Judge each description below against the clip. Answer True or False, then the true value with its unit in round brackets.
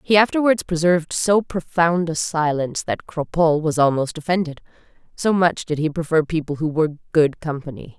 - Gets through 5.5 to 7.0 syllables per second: False (5.3 syllables/s)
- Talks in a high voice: False (160 Hz)